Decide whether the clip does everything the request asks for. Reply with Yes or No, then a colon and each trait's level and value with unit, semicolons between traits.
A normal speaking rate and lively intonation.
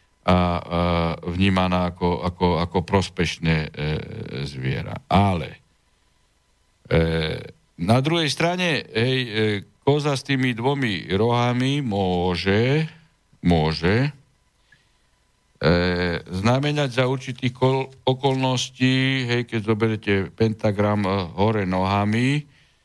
No: slow, 95 wpm; wide, 6.5 semitones